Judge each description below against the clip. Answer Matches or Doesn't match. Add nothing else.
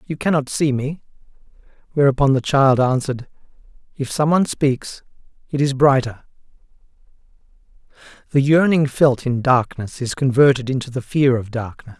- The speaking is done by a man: Matches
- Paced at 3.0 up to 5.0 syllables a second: Doesn't match